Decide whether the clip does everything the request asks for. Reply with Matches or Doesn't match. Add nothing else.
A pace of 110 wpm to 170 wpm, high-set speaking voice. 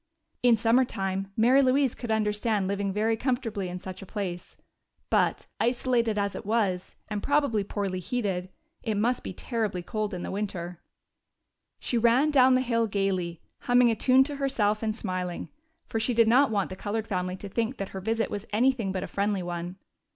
Doesn't match